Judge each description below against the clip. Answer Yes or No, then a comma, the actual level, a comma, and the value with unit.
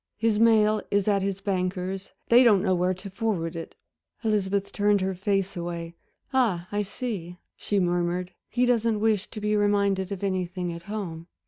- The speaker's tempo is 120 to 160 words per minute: No, average, 175 wpm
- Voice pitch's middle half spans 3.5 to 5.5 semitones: No, narrow, 2.6 semitones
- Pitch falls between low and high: No, high, 195 Hz